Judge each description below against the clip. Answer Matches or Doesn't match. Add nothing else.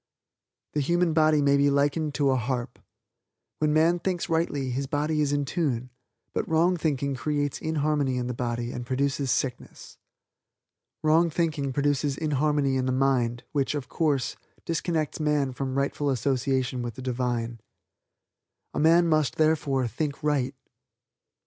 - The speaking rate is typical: Matches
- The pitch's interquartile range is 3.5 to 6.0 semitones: Doesn't match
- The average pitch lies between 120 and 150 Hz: Matches